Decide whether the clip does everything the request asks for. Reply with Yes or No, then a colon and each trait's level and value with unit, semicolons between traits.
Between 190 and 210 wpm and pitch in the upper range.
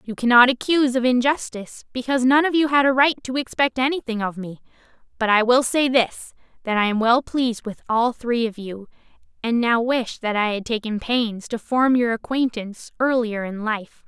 Yes: average, 200 wpm; high, 240 Hz